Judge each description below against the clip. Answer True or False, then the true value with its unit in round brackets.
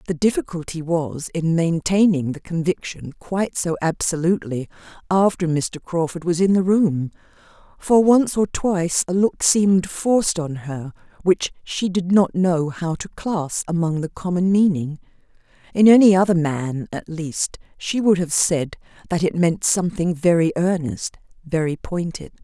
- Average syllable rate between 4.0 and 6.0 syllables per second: True (4.5 syllables/s)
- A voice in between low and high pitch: True (170 Hz)